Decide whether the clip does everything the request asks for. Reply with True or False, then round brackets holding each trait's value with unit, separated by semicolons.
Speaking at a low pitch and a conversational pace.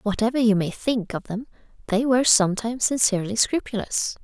False (225 Hz; 155 wpm)